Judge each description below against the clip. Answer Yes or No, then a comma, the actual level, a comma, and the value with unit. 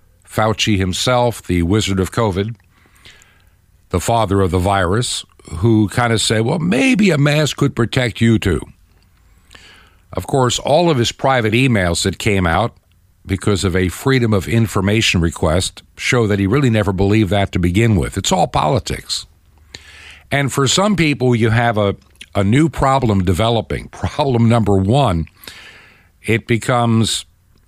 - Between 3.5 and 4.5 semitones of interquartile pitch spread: Yes, average, 4.2 semitones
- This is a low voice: Yes, low, 105 Hz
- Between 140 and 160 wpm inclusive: Yes, average, 150 wpm